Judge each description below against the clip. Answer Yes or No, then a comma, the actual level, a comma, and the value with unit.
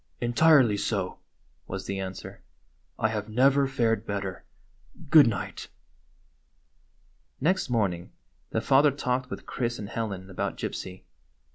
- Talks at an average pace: No, slow, 120 wpm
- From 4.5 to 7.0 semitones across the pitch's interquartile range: Yes, average, 5.1 semitones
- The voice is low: Yes, low, 115 Hz